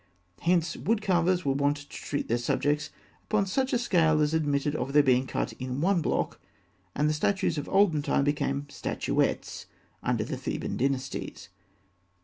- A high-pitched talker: No, medium, 150 Hz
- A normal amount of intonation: Yes, average, 4.2 semitones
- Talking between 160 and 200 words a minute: Yes, average, 165 wpm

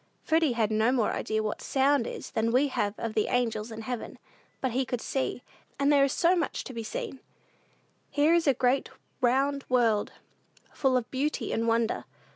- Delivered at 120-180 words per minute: No, average, 190 wpm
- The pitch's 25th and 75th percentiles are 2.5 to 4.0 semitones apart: Yes, average, 3.5 semitones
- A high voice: Yes, very high, 250 Hz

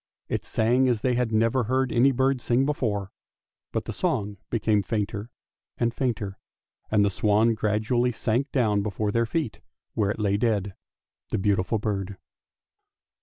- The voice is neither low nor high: No, low, 110 Hz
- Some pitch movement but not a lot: Yes, average, 3.1 semitones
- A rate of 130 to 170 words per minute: Yes, average, 160 wpm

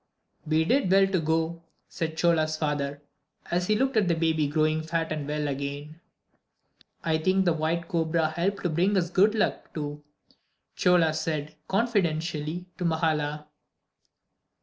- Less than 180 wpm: Yes, average, 150 wpm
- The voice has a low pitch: No, medium, 160 Hz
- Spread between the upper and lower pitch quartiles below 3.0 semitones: Yes, narrow, 2.5 semitones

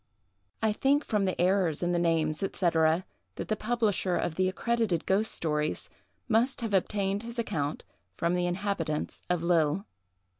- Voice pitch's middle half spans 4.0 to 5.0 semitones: Yes, average, 4.3 semitones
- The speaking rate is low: No, average, 155 wpm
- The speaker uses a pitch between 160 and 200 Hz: Yes, medium, 185 Hz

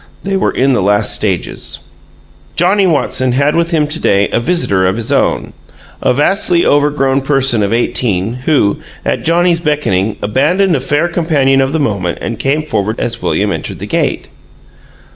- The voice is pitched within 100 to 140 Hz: Yes, low, 135 Hz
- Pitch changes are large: Yes, wide, 6.6 semitones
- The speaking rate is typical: Yes, average, 170 wpm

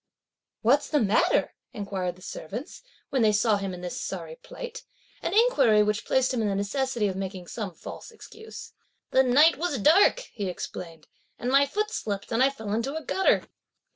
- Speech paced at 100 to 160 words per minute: No, average, 185 wpm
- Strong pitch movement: Yes, wide, 6.0 semitones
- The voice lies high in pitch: Yes, high, 225 Hz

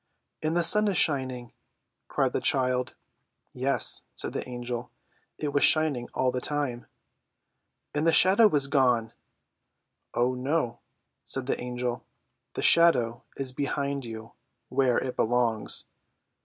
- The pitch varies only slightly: No, average, 3.1 semitones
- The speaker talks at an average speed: No, slow, 130 wpm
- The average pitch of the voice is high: No, low, 130 Hz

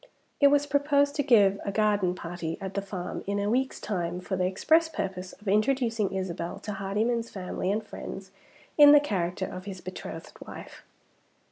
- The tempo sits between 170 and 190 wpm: Yes, average, 175 wpm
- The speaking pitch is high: Yes, high, 200 Hz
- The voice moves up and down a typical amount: Yes, average, 4.7 semitones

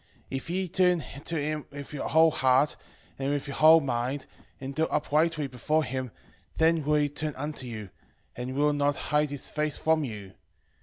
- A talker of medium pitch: Yes, medium, 145 Hz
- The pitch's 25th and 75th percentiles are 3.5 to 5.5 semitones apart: No, average, 2.7 semitones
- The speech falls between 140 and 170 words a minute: No, average, 190 wpm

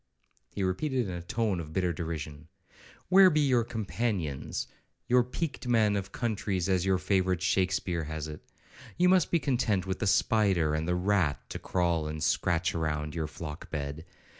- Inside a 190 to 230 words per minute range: No, average, 170 wpm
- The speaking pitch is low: Yes, very low, 95 Hz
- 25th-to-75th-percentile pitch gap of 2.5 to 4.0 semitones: No, wide, 5.5 semitones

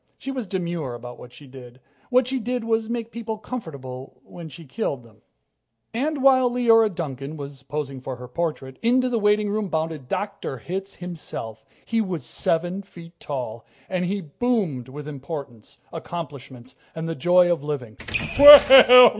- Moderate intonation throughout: No, wide, 8.2 semitones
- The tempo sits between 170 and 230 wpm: No, average, 155 wpm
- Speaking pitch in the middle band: Yes, medium, 165 Hz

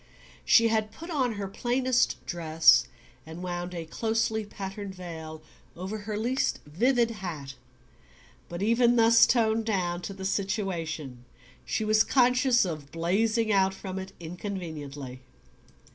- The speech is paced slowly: Yes, slow, 130 wpm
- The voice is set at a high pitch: Yes, high, 195 Hz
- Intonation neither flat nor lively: Yes, average, 4.9 semitones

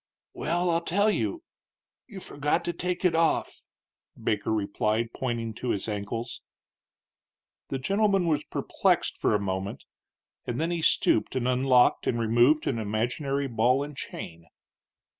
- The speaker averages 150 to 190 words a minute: No, average, 140 wpm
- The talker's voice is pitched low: Yes, low, 130 Hz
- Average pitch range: No, wide, 6.8 semitones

